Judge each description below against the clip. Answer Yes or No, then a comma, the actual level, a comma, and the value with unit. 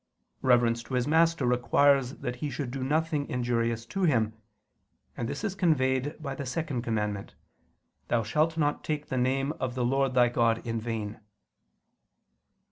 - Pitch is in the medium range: No, low, 130 Hz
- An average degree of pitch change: Yes, average, 3.7 semitones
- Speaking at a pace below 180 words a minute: Yes, average, 160 wpm